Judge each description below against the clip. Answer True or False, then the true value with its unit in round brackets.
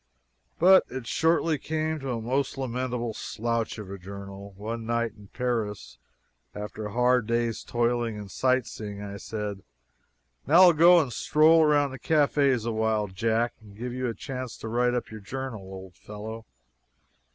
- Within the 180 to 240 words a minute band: False (160 wpm)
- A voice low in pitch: True (115 Hz)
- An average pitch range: True (3.9 semitones)